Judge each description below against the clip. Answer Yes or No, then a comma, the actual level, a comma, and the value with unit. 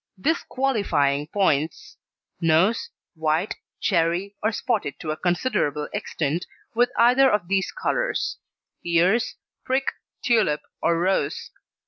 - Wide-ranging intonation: Yes, wide, 6.7 semitones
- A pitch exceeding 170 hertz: Yes, medium, 185 Hz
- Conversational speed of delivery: No, slow, 105 wpm